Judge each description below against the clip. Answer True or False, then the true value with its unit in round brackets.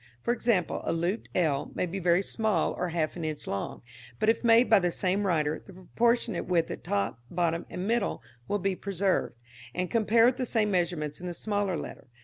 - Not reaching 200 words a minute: False (205 wpm)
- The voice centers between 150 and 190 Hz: True (185 Hz)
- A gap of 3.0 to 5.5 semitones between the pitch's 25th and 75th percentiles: True (4.2 semitones)